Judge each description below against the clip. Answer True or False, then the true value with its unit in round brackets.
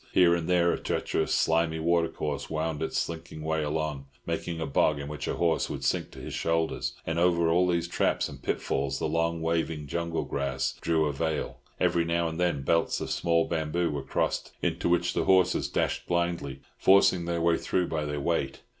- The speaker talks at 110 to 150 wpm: False (200 wpm)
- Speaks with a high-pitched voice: False (80 Hz)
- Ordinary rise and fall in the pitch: False (1.8 semitones)